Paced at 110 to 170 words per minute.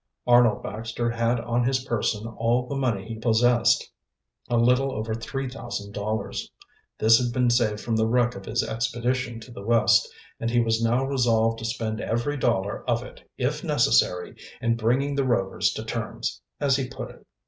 No: average, 180 wpm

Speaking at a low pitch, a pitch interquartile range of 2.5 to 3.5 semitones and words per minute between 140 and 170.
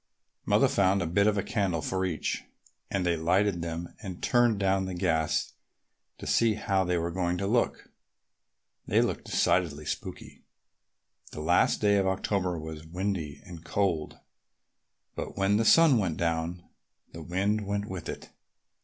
Yes: very low, 95 Hz; average, 3.0 semitones; average, 155 wpm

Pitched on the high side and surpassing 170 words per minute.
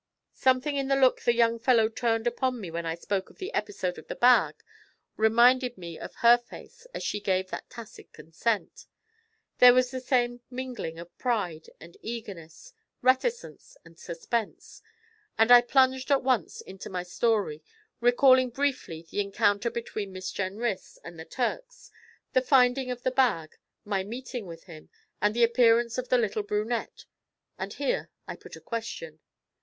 No: high, 235 Hz; average, 165 wpm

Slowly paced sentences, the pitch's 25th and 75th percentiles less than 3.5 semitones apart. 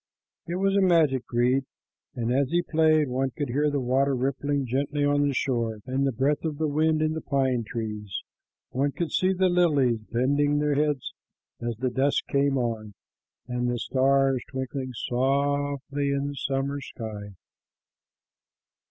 No: average, 160 wpm; narrow, 2.5 semitones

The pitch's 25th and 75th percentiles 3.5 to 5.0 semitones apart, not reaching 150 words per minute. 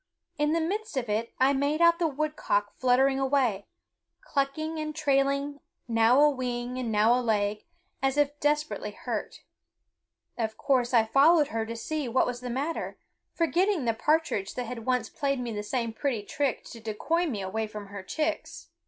No: average, 4.6 semitones; average, 180 wpm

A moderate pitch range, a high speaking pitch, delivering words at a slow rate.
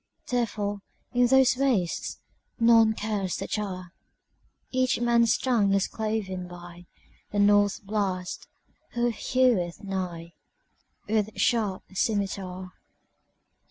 Yes: average, 3.9 semitones; high, 205 Hz; slow, 85 wpm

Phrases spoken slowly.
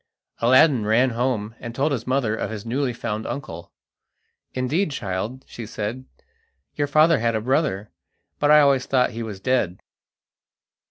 No: average, 155 wpm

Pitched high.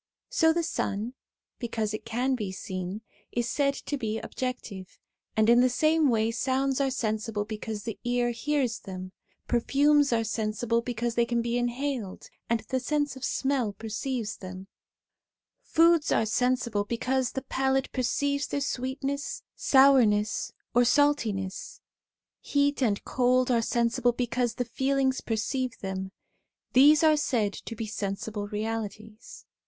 Yes: high, 240 Hz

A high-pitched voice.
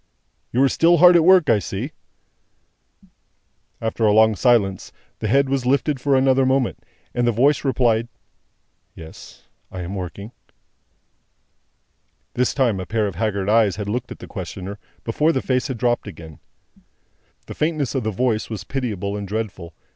No: low, 115 Hz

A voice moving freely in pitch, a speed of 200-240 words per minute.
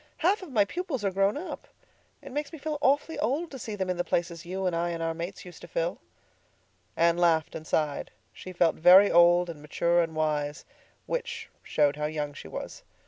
Yes: wide, 8.5 semitones; fast, 205 wpm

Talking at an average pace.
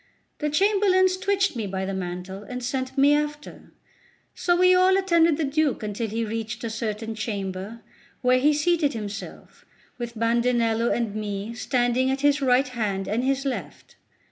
Yes: average, 165 wpm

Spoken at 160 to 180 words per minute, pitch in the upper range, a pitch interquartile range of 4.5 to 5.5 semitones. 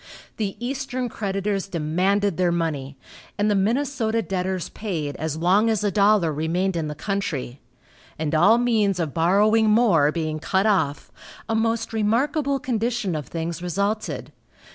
No: average, 145 wpm; high, 195 Hz; average, 5.1 semitones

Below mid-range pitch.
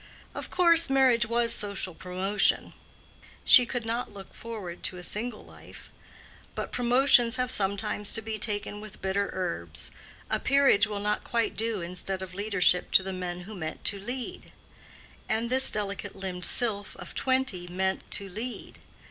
No: high, 205 Hz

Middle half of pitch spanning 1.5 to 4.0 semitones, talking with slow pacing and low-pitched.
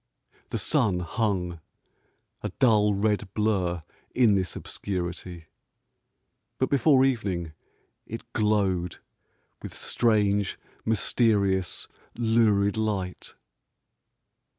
Yes: average, 3.4 semitones; slow, 80 wpm; low, 100 Hz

